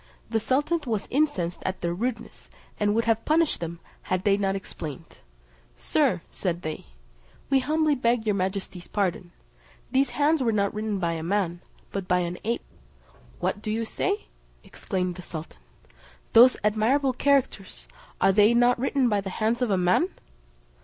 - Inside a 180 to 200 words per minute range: No, average, 165 wpm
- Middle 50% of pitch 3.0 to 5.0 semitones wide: No, wide, 5.4 semitones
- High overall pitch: Yes, high, 210 Hz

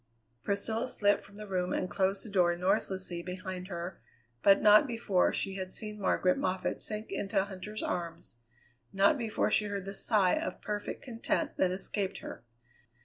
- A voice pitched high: Yes, high, 195 Hz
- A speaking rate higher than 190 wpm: No, average, 165 wpm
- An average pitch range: No, narrow, 2.3 semitones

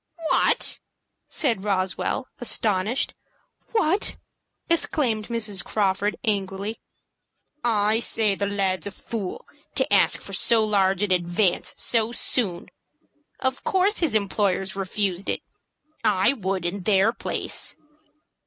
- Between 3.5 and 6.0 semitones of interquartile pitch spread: No, average, 3.1 semitones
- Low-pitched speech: No, high, 205 Hz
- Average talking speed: No, slow, 115 wpm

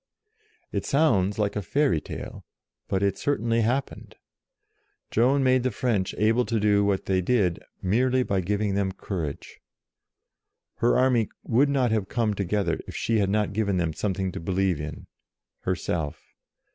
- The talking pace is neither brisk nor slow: Yes, average, 160 wpm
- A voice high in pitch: No, low, 105 Hz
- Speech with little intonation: No, average, 4.1 semitones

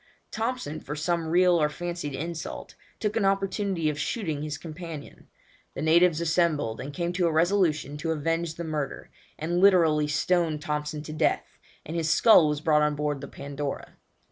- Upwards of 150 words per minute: Yes, average, 170 wpm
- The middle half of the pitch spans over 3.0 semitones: No, average, 2.7 semitones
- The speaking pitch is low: No, medium, 160 Hz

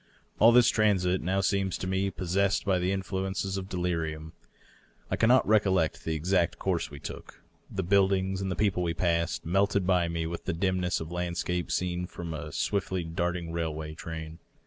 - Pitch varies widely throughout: No, narrow, 2.4 semitones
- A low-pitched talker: Yes, very low, 90 Hz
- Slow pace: No, average, 180 wpm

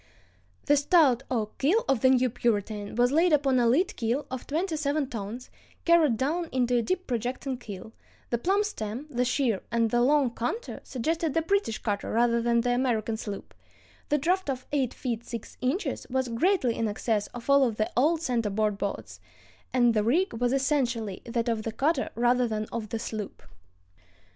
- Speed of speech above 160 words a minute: Yes, average, 185 wpm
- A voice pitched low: No, high, 245 Hz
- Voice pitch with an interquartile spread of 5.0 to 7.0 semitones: No, average, 4.1 semitones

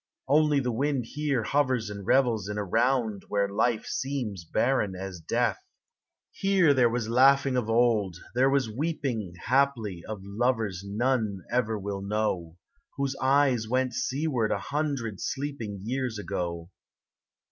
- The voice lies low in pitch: Yes, low, 120 Hz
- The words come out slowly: No, average, 145 wpm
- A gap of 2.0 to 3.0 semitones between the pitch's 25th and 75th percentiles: No, average, 4.7 semitones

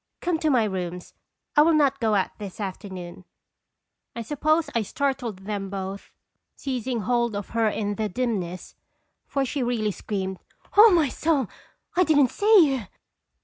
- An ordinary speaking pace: Yes, average, 155 wpm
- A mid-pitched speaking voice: No, high, 230 Hz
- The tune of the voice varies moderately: No, wide, 6.1 semitones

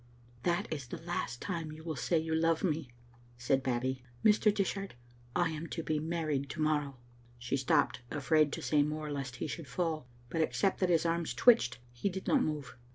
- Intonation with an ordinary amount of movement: Yes, average, 3.5 semitones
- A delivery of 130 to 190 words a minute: No, average, 200 wpm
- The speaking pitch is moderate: Yes, medium, 155 Hz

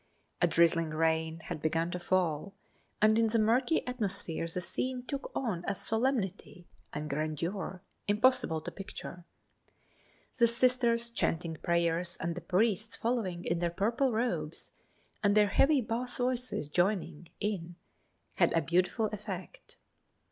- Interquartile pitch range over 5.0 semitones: Yes, wide, 5.6 semitones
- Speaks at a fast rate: No, slow, 135 wpm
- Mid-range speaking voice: No, high, 195 Hz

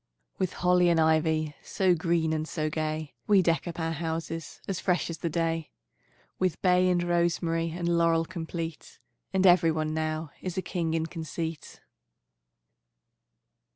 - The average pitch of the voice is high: No, medium, 165 Hz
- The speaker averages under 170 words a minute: Yes, average, 155 wpm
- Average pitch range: No, narrow, 1.6 semitones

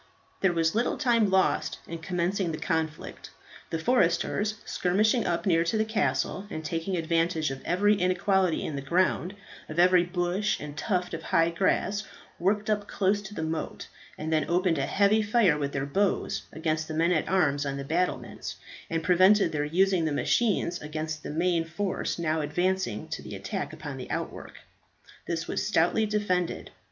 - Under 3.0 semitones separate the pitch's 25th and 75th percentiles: No, average, 3.6 semitones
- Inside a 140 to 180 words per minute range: Yes, average, 175 wpm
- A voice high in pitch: No, medium, 175 Hz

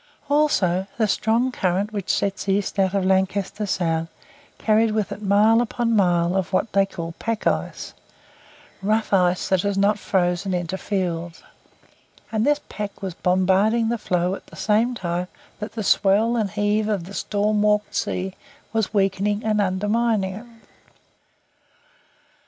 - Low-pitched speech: No, high, 200 Hz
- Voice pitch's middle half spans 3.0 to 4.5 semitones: No, narrow, 2.5 semitones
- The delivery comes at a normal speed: Yes, average, 150 wpm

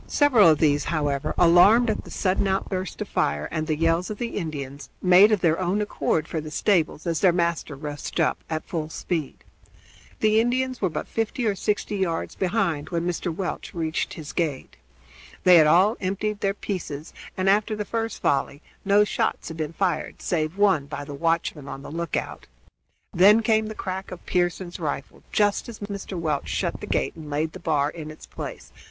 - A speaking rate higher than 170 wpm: Yes, average, 195 wpm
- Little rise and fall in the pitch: No, average, 4.6 semitones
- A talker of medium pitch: Yes, medium, 175 Hz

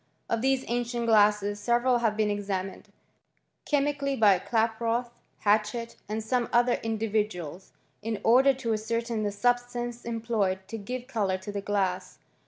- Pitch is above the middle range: Yes, high, 225 Hz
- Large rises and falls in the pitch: No, average, 2.8 semitones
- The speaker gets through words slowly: No, average, 150 wpm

